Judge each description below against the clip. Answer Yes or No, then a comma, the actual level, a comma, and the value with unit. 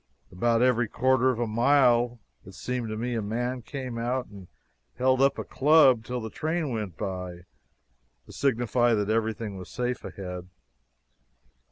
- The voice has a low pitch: Yes, low, 120 Hz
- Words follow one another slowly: No, average, 160 wpm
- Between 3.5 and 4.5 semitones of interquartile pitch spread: No, average, 2.8 semitones